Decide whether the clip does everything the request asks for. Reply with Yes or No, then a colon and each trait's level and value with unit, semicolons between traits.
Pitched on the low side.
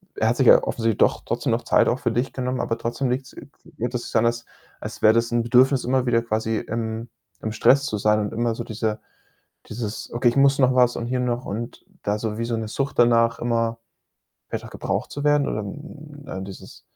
Yes: low, 120 Hz